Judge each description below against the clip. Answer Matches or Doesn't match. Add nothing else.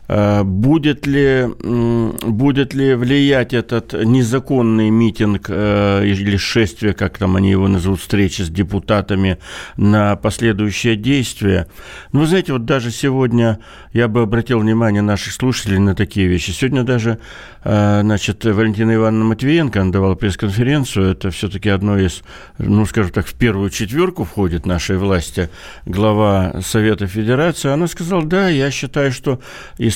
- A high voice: Doesn't match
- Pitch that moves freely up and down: Doesn't match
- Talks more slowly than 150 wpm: Matches